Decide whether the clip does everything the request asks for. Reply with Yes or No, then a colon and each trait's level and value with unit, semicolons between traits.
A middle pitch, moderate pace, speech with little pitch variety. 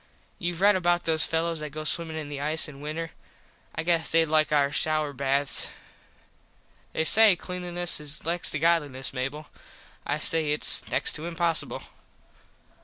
Yes: medium, 160 Hz; average, 160 wpm; narrow, 2.3 semitones